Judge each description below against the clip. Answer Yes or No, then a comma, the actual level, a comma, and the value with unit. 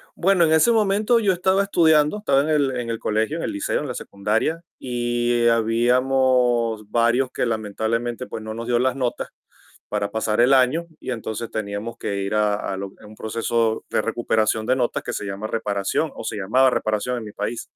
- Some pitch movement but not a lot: Yes, average, 3.6 semitones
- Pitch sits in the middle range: No, low, 120 Hz